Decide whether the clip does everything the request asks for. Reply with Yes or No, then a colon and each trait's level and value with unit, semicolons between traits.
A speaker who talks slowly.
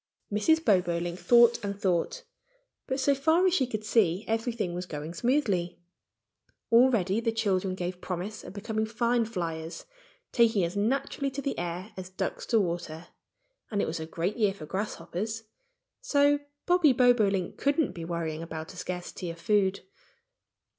No: average, 155 wpm